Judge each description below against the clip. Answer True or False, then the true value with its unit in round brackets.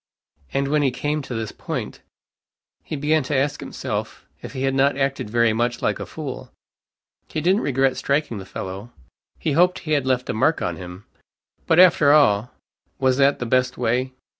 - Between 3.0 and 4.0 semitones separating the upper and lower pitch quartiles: True (3.3 semitones)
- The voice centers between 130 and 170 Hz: True (135 Hz)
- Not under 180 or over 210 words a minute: True (190 wpm)